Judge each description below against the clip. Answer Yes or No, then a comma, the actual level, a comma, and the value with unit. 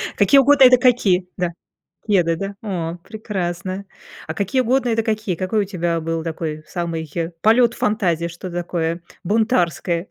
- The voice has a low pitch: No, medium, 185 Hz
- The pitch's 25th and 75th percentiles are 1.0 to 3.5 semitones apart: No, average, 4.6 semitones